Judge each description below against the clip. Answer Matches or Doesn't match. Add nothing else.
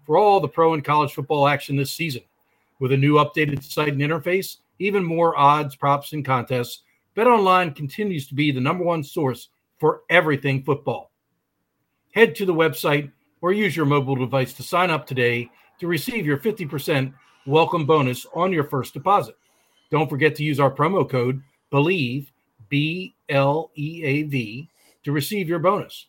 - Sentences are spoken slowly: Doesn't match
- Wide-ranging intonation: Doesn't match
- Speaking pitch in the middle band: Matches